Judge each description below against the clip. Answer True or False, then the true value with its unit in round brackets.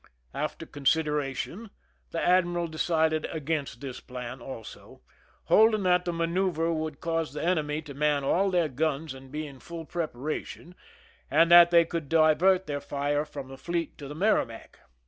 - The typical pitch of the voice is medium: True (155 Hz)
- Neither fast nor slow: True (160 wpm)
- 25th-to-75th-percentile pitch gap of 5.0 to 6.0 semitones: False (3.1 semitones)